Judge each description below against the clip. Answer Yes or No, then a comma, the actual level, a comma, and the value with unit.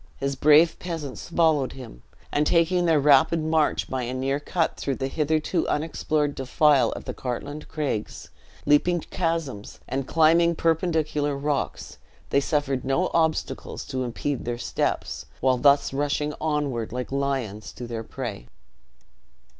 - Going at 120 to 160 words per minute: Yes, average, 140 wpm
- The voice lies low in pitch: No, medium, 145 Hz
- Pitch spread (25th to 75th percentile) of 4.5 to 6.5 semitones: No, average, 3.2 semitones